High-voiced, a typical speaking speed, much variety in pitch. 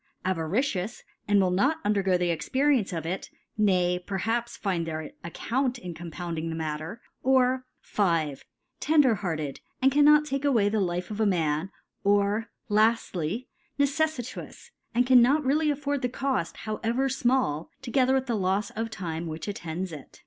Yes: high, 205 Hz; average, 160 wpm; wide, 6.8 semitones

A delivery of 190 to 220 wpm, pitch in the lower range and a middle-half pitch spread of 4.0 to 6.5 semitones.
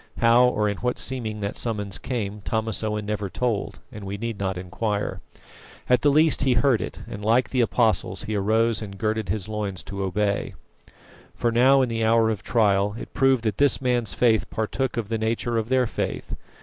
No: average, 200 wpm; low, 110 Hz; average, 2.7 semitones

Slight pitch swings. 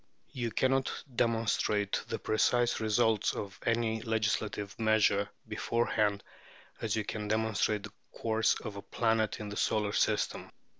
Yes: narrow, 1.5 semitones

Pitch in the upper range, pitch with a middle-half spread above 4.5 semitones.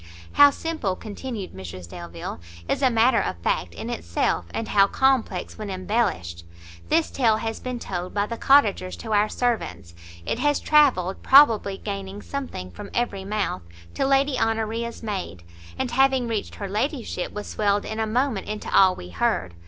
Yes: high, 215 Hz; average, 5.2 semitones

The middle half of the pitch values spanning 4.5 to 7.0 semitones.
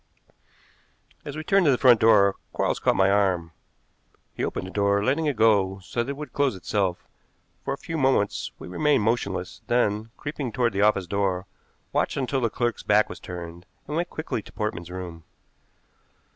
Yes: wide, 5.6 semitones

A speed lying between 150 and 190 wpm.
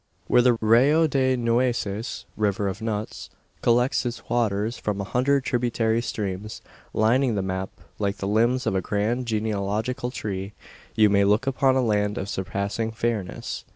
Yes: average, 155 wpm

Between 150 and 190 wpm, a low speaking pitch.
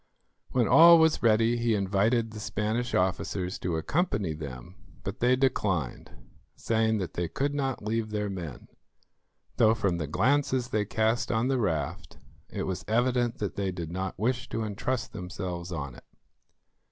Yes: average, 160 wpm; low, 110 Hz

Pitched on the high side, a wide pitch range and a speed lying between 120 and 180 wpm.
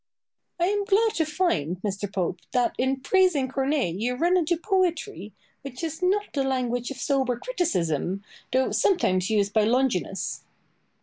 Yes: very high, 265 Hz; wide, 8.7 semitones; average, 160 wpm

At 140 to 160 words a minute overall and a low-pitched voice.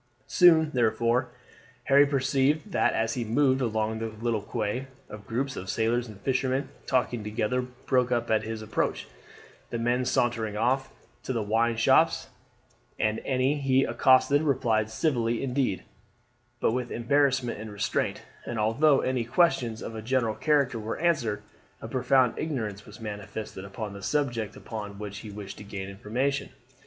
Yes: average, 155 wpm; low, 120 Hz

